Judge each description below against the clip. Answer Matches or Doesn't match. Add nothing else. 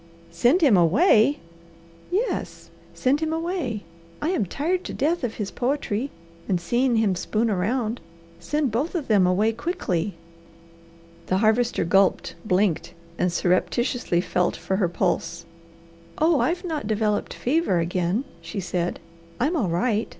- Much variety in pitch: Matches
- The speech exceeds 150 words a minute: Doesn't match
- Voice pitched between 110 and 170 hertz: Doesn't match